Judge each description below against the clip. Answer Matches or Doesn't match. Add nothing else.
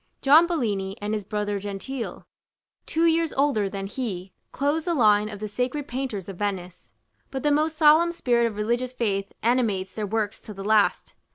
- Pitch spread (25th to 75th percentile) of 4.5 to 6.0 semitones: Matches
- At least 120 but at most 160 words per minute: Doesn't match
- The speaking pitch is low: Doesn't match